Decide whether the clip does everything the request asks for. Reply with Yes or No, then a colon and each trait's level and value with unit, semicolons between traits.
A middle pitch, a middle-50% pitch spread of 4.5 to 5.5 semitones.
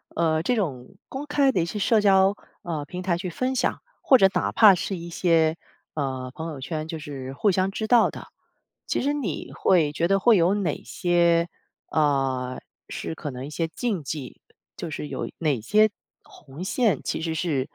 Yes: medium, 170 Hz; average, 4.8 semitones